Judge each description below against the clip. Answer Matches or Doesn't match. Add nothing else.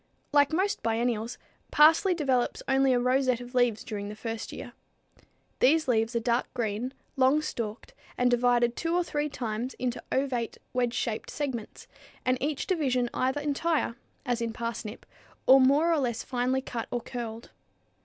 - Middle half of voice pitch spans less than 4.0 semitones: Matches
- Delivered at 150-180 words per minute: Matches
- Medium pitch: Doesn't match